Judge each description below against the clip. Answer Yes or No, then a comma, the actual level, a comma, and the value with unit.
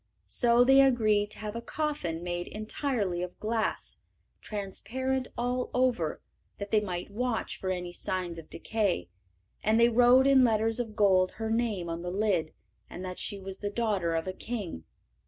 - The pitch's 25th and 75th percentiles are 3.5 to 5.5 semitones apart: Yes, average, 4.6 semitones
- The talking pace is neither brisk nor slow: Yes, average, 175 wpm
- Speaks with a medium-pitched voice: No, high, 210 Hz